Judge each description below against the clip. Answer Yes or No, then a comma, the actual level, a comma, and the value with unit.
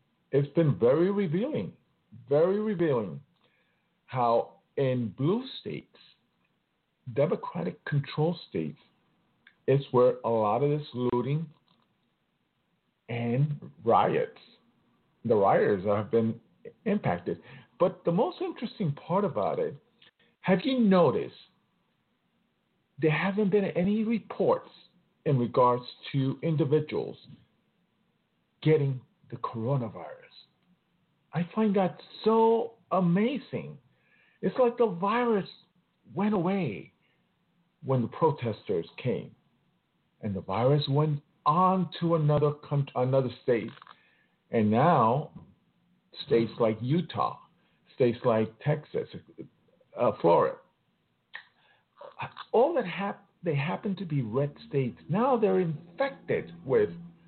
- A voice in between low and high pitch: Yes, medium, 165 Hz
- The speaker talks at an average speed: No, slow, 95 wpm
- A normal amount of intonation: No, wide, 6.6 semitones